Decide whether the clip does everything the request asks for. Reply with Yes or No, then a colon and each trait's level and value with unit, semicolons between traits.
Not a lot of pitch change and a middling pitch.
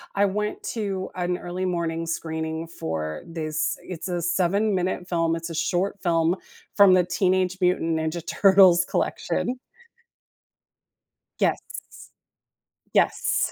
Yes: narrow, 2.2 semitones; medium, 175 Hz